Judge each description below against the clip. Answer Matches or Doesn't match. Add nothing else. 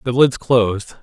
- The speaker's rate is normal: Matches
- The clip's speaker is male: Matches